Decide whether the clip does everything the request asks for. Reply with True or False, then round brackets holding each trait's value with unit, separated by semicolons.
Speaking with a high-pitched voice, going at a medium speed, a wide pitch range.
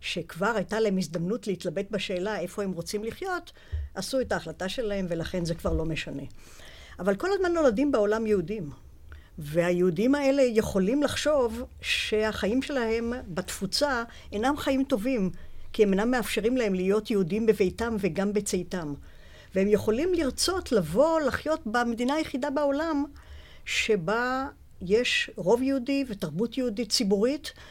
True (215 Hz; 130 wpm; 5.9 semitones)